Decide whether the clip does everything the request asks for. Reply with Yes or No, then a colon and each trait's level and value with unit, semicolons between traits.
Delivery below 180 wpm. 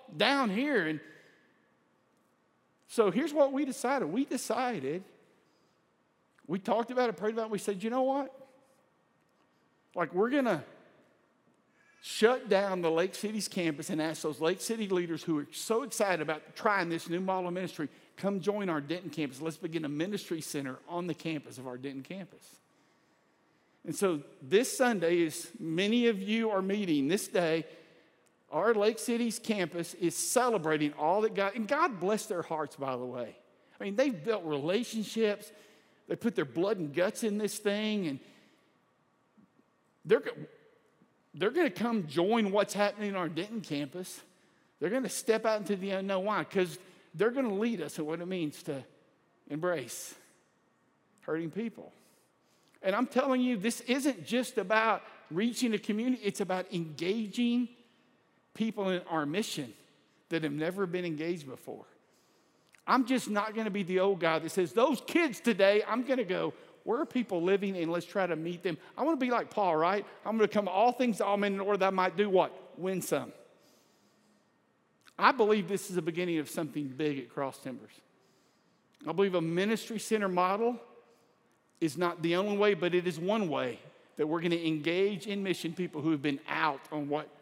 No: average, 185 wpm